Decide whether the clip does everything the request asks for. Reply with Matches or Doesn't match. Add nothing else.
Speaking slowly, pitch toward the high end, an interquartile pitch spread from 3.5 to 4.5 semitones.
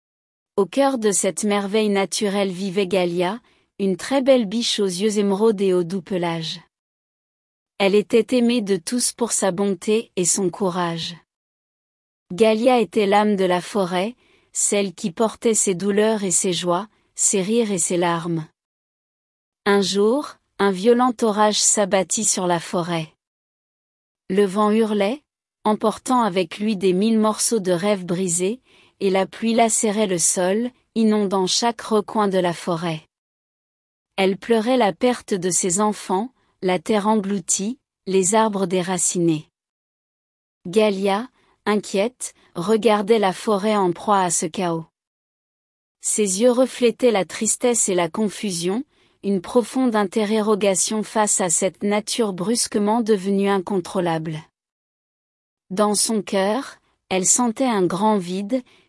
Doesn't match